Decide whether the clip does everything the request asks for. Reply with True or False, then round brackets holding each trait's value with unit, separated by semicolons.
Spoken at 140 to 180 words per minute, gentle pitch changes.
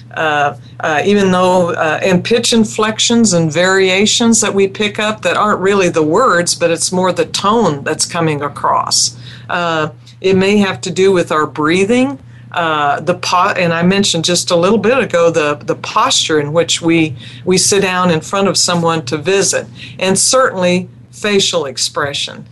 False (175 wpm; 3.8 semitones)